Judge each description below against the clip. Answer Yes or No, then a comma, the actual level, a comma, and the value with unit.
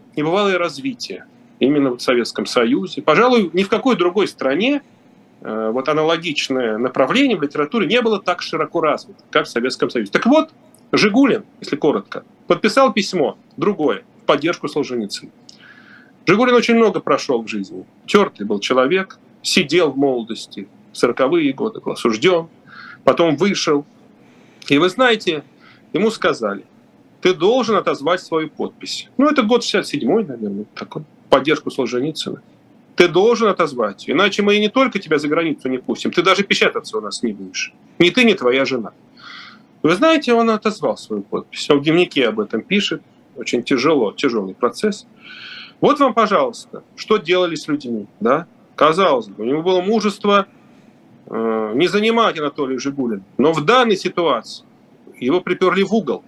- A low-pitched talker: No, high, 190 Hz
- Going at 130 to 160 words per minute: Yes, average, 150 wpm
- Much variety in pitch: Yes, wide, 7.8 semitones